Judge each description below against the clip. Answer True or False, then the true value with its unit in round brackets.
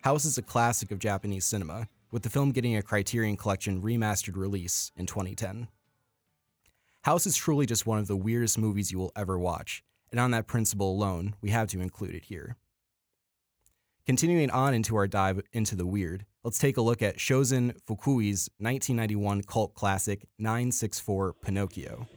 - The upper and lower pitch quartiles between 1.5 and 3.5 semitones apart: True (3.1 semitones)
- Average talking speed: True (170 wpm)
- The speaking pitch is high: False (110 Hz)